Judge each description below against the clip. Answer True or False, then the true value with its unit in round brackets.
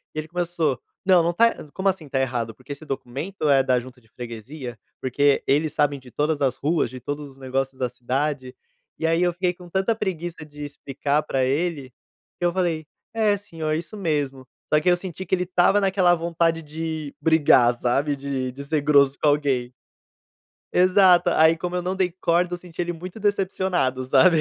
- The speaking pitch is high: False (155 Hz)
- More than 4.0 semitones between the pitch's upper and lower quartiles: True (4.6 semitones)